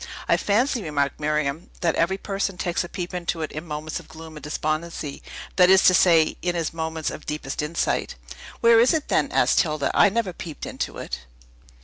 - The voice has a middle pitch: Yes, medium, 165 Hz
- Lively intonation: No, average, 3.3 semitones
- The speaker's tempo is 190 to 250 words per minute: Yes, average, 200 wpm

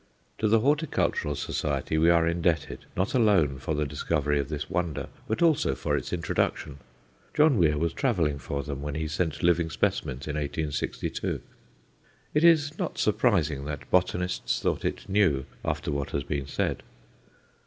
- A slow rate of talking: No, average, 160 wpm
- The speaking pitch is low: Yes, very low, 80 Hz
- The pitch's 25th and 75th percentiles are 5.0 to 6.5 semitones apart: Yes, wide, 5.4 semitones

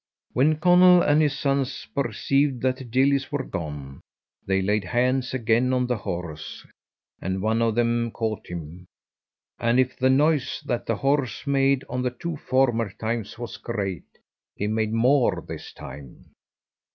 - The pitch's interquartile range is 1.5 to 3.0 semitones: No, average, 4.1 semitones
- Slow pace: No, average, 155 wpm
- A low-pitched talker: Yes, low, 120 Hz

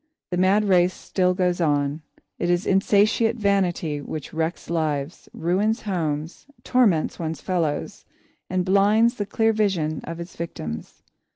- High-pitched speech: No, medium, 180 Hz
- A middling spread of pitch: Yes, average, 4.0 semitones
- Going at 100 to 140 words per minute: Yes, slow, 135 wpm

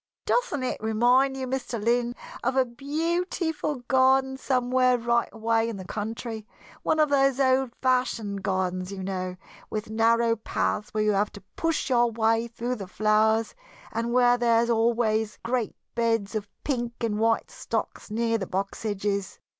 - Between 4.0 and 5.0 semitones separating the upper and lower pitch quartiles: No, average, 2.9 semitones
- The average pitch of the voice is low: No, high, 230 Hz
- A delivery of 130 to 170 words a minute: Yes, average, 160 wpm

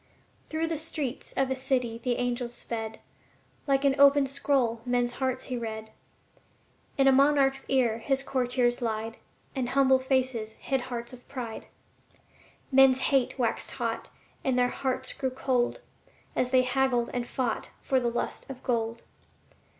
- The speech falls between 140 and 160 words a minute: Yes, average, 150 wpm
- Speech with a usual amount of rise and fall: No, narrow, 1.9 semitones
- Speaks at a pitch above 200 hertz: Yes, very high, 255 Hz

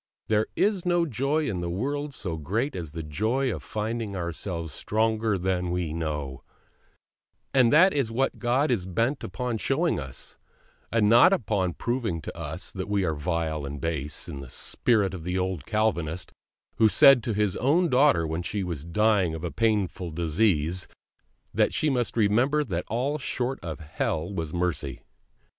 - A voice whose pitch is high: No, low, 100 Hz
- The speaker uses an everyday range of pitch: No, wide, 6.3 semitones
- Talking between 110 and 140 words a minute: No, average, 170 wpm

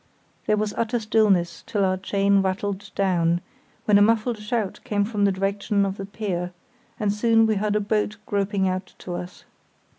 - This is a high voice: Yes, high, 200 Hz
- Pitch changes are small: Yes, narrow, 1.9 semitones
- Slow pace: No, average, 180 wpm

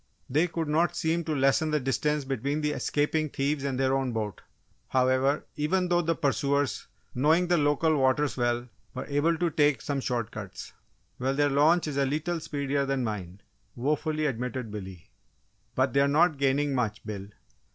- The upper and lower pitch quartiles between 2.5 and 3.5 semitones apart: Yes, average, 2.9 semitones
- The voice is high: No, medium, 140 Hz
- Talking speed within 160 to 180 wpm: Yes, average, 175 wpm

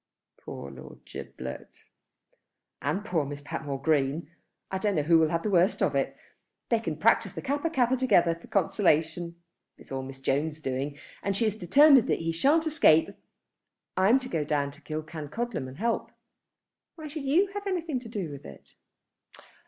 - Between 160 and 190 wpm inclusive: Yes, average, 175 wpm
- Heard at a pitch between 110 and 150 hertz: No, medium, 170 Hz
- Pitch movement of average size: No, wide, 8.4 semitones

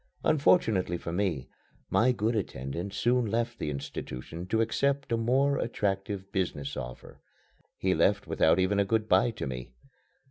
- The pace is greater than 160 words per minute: No, average, 150 wpm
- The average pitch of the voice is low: Yes, low, 100 Hz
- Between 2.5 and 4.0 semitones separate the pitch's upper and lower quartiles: No, wide, 5.5 semitones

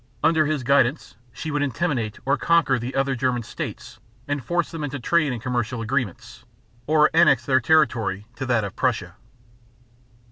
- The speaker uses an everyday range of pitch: Yes, average, 4.2 semitones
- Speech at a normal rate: Yes, average, 165 wpm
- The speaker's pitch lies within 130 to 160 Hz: Yes, low, 135 Hz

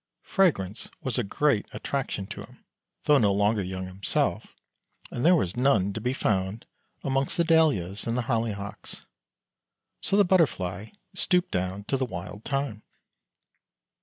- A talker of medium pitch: No, low, 110 Hz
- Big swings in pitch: Yes, wide, 6.1 semitones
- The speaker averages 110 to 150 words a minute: Yes, average, 145 wpm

